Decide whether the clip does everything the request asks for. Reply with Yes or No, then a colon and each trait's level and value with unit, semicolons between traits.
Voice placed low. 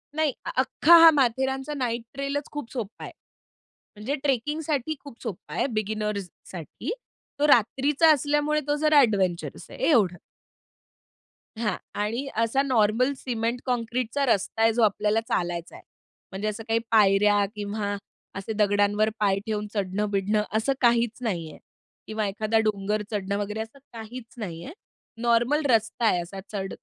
No: high, 225 Hz